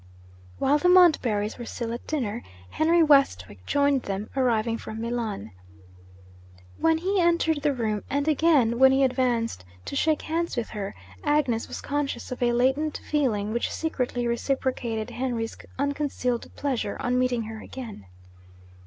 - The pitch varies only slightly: No, average, 4.2 semitones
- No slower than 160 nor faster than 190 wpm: No, average, 145 wpm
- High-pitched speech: Yes, very high, 255 Hz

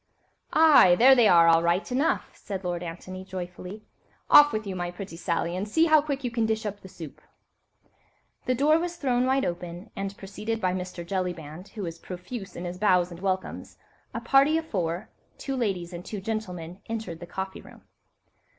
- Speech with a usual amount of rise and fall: Yes, average, 4.8 semitones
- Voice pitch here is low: No, high, 190 Hz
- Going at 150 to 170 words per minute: No, average, 185 wpm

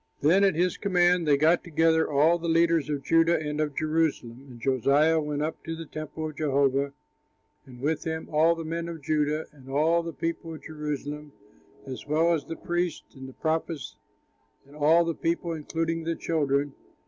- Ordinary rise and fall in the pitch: No, narrow, 2.2 semitones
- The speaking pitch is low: No, medium, 155 Hz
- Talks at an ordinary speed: Yes, average, 185 wpm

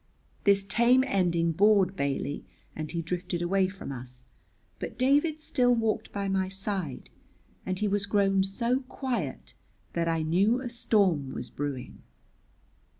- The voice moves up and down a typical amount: Yes, average, 4.8 semitones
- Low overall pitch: No, high, 195 Hz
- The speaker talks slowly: No, average, 145 wpm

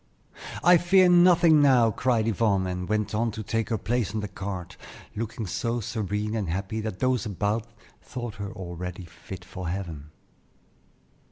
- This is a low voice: Yes, low, 105 Hz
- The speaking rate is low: No, average, 165 wpm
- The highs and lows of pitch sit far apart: No, average, 3.8 semitones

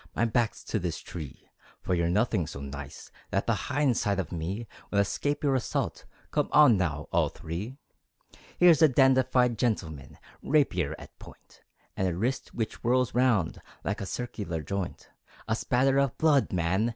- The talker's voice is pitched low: Yes, low, 110 Hz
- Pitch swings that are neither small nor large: No, wide, 6.8 semitones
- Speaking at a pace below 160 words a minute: No, average, 165 wpm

